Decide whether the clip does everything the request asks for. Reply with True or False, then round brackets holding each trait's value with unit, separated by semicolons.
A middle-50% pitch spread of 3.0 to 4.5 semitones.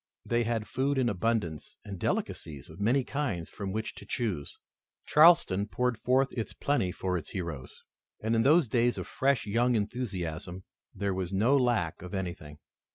False (5.4 semitones)